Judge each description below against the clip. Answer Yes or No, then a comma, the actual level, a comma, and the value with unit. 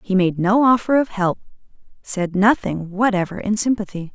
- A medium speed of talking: Yes, average, 160 wpm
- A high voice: Yes, high, 200 Hz